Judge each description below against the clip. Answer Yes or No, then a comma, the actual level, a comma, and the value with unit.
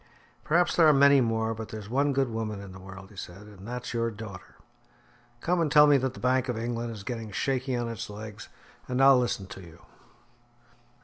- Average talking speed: No, fast, 210 wpm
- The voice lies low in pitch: Yes, low, 115 Hz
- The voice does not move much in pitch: No, average, 4.0 semitones